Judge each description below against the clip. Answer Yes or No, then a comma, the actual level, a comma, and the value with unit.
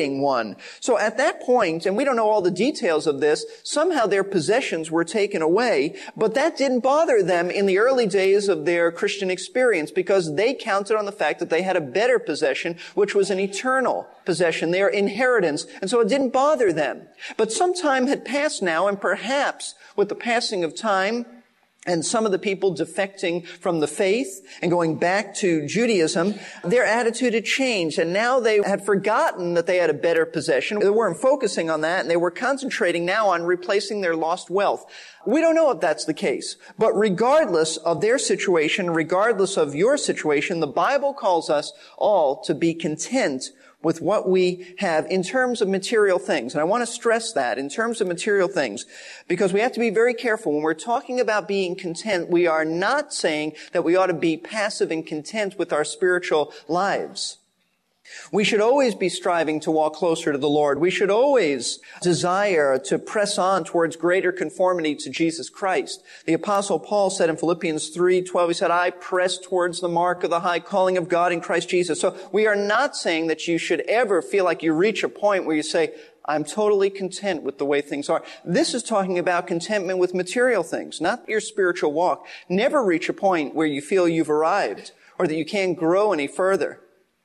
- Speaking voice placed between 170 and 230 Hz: Yes, high, 190 Hz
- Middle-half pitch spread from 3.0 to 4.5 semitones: No, average, 4.9 semitones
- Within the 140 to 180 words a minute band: No, average, 200 wpm